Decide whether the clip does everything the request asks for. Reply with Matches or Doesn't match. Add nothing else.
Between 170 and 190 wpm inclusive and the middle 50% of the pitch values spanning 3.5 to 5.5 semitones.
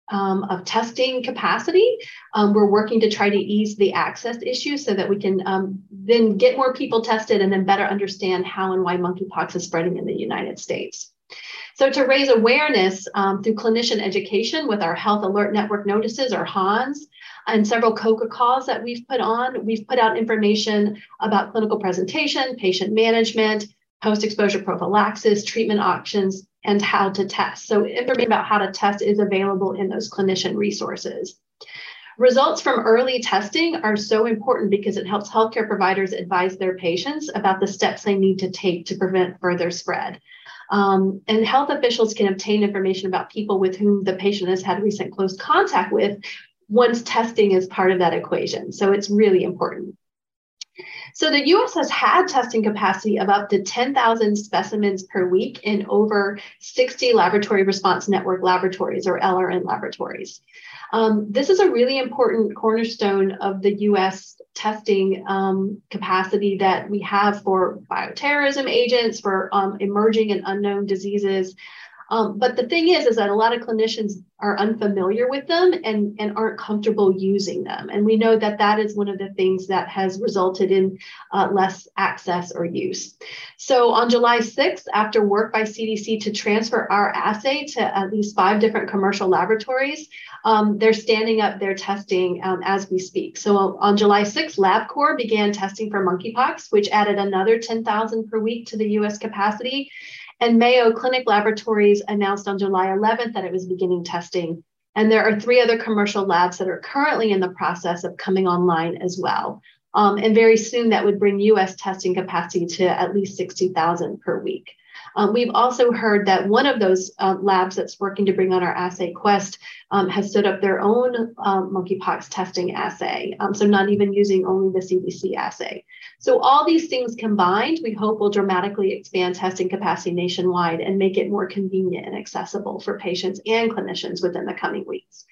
Doesn't match